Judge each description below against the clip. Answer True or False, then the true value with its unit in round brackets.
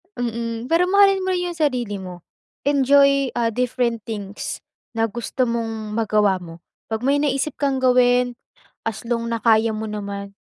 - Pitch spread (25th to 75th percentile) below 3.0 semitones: False (3.9 semitones)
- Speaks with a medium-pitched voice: False (235 Hz)